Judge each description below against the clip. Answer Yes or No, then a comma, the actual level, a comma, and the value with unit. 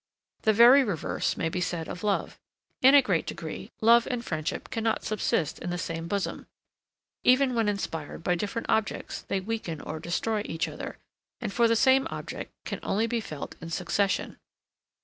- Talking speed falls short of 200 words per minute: Yes, average, 175 wpm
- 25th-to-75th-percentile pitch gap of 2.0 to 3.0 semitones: No, average, 5.2 semitones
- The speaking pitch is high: Yes, high, 205 Hz